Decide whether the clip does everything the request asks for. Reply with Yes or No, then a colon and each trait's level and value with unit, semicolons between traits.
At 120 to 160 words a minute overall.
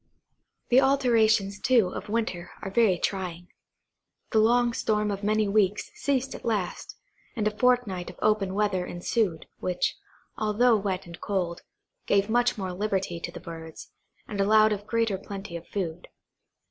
Yes: average, 155 wpm